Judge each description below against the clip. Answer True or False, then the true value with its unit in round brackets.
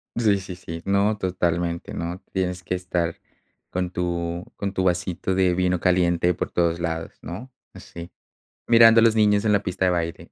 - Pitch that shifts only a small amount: True (2.2 semitones)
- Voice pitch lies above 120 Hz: False (90 Hz)